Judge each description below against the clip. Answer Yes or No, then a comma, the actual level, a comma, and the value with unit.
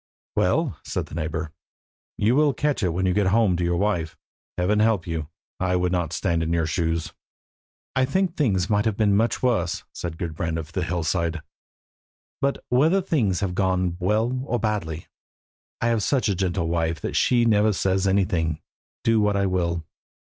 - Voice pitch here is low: Yes, very low, 95 Hz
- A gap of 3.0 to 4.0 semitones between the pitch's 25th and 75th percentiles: No, average, 4.5 semitones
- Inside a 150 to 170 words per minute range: No, average, 180 wpm